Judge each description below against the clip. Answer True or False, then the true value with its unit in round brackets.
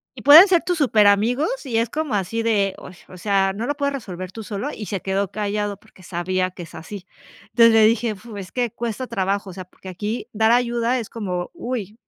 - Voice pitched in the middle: False (215 Hz)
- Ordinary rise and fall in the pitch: True (3.7 semitones)